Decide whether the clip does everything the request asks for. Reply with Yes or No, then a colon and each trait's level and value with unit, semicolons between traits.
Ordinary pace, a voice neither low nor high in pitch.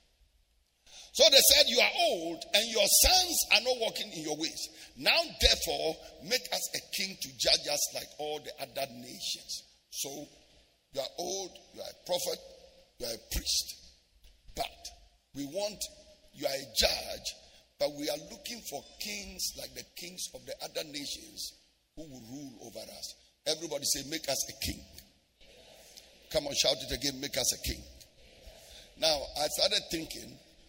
Yes: average, 165 wpm; medium, 160 Hz